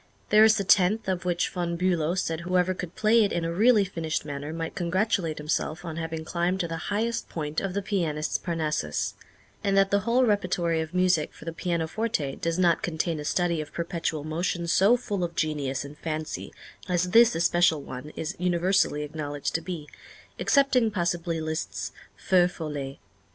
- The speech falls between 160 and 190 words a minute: Yes, average, 180 wpm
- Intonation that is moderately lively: Yes, average, 3.1 semitones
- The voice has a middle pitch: Yes, medium, 170 Hz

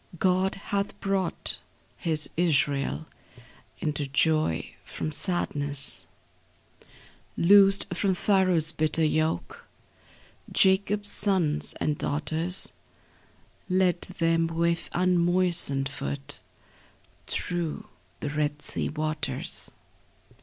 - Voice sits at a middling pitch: Yes, medium, 165 Hz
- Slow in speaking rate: Yes, slow, 80 wpm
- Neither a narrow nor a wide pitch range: Yes, average, 3.6 semitones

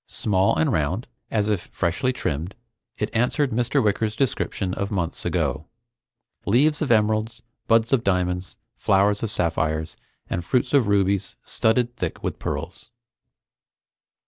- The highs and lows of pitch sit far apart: No, average, 4.3 semitones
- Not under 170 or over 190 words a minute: No, slow, 135 wpm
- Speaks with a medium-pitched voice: No, low, 105 Hz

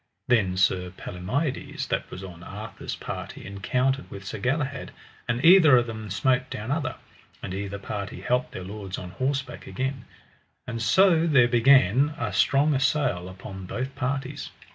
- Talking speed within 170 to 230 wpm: No, average, 150 wpm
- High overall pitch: No, low, 125 Hz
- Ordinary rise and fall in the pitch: No, wide, 5.9 semitones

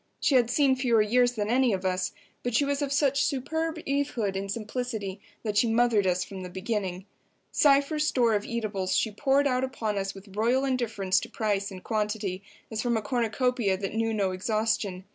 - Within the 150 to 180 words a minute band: No, average, 195 wpm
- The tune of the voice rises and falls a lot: No, average, 4.3 semitones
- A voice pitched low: No, high, 225 Hz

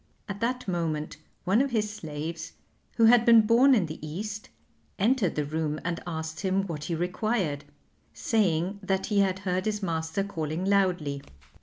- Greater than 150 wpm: Yes, average, 165 wpm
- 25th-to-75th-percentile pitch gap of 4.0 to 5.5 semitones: Yes, average, 4.8 semitones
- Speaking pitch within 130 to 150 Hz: No, medium, 185 Hz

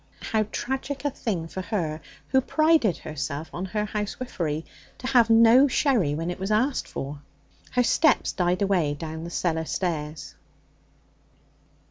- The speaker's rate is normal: Yes, average, 145 wpm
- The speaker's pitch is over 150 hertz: Yes, high, 190 Hz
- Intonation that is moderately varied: No, wide, 7.3 semitones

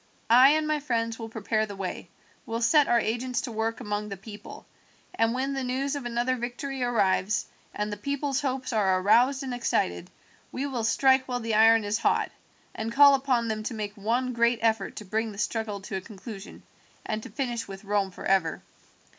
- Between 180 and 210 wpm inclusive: Yes, average, 195 wpm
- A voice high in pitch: Yes, high, 230 Hz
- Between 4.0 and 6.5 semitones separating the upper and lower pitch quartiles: No, average, 3.5 semitones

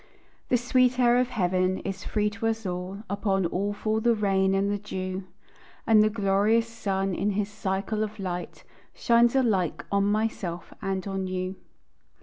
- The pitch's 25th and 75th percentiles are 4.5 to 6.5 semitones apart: No, narrow, 2.6 semitones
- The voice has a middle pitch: No, high, 200 Hz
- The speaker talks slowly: No, average, 165 wpm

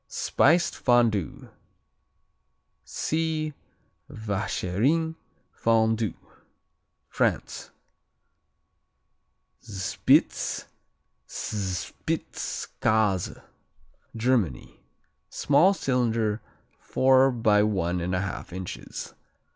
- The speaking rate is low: Yes, slow, 55 wpm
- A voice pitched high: No, low, 110 Hz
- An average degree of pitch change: Yes, average, 4.9 semitones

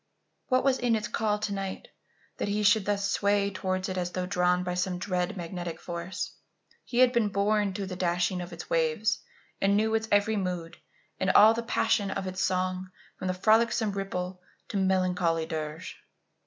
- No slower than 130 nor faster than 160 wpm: No, average, 180 wpm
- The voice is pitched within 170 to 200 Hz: Yes, high, 190 Hz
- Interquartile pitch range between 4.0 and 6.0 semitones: No, narrow, 2.5 semitones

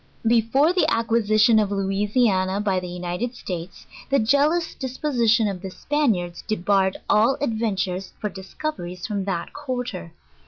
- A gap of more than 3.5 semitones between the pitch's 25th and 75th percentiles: Yes, average, 4.5 semitones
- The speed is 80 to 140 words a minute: Yes, slow, 135 wpm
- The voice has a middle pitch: No, high, 215 Hz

